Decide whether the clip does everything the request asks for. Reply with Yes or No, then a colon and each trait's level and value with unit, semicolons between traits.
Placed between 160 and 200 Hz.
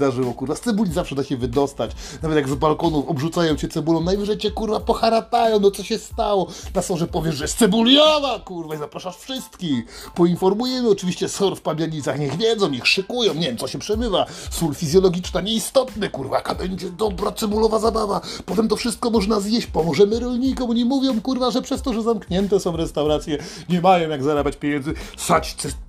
Yes: high, 190 Hz